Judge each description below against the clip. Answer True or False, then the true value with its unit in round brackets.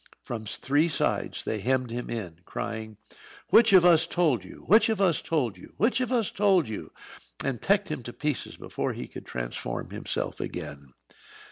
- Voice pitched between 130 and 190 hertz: True (135 Hz)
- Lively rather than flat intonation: True (8.9 semitones)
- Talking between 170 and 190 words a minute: True (175 wpm)